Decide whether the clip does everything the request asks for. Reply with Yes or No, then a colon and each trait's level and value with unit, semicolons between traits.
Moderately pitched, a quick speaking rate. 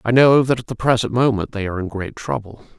No: low, 115 Hz; fast, 260 wpm